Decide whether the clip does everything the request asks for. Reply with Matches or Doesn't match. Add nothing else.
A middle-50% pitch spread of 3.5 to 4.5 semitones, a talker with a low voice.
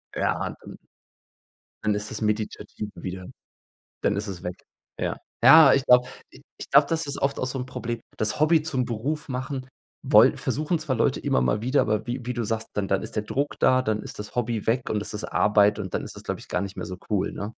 Matches